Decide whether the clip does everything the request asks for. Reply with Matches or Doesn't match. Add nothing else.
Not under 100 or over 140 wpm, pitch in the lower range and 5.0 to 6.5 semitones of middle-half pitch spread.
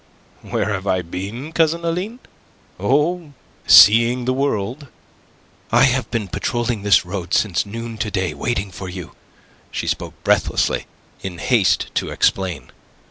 Matches